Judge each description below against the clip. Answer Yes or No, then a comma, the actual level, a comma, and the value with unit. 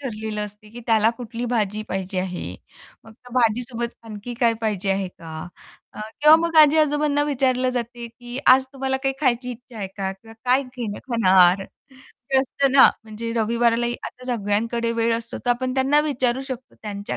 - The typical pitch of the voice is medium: No, high, 235 Hz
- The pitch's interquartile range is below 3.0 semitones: No, average, 3.3 semitones